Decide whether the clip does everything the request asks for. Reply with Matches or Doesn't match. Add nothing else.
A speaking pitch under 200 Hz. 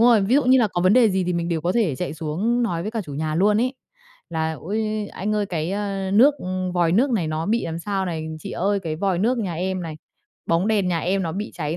Matches